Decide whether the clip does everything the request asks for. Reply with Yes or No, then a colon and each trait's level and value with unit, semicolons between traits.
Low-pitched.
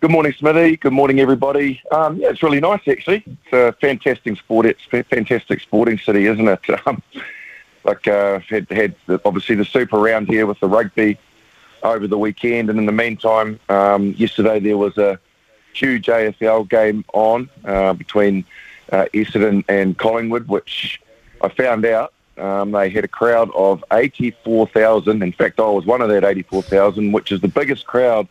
Yes: low, 110 Hz